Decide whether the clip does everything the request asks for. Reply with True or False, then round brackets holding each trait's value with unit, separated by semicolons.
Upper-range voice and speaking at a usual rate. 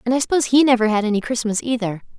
False (235 Hz; 245 wpm)